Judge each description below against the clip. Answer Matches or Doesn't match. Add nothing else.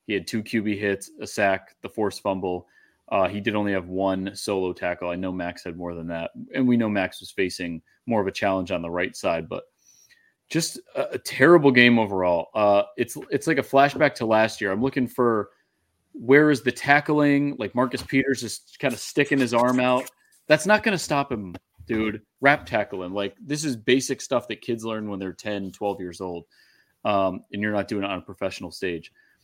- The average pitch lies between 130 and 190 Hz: Doesn't match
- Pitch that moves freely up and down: Matches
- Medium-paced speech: Doesn't match